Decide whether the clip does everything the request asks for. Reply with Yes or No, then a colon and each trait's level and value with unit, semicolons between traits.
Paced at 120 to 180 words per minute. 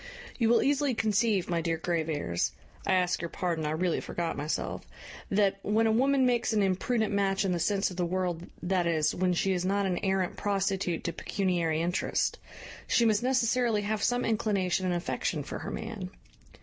No: average, 190 wpm